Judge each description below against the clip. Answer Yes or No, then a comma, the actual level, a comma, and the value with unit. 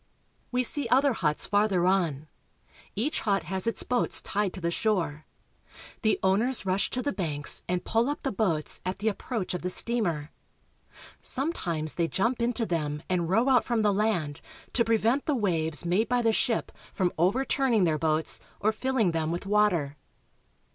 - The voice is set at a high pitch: Yes, high, 200 Hz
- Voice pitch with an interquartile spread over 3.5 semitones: Yes, wide, 5.6 semitones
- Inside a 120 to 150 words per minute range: No, average, 175 wpm